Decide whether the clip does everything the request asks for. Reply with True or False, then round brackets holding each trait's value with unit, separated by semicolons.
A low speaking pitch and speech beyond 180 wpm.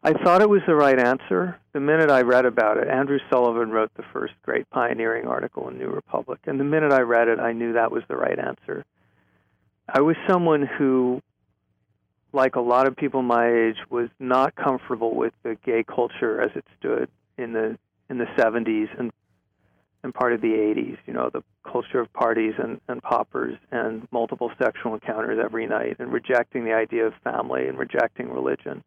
True (120 Hz; 195 wpm)